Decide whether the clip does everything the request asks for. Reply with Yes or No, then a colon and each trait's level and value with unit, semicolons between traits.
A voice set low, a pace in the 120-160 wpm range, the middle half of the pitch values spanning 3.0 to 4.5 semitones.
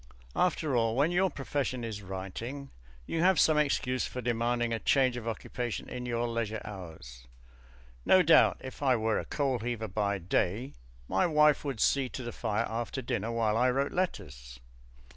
No: low, 120 Hz; average, 175 wpm; average, 3.8 semitones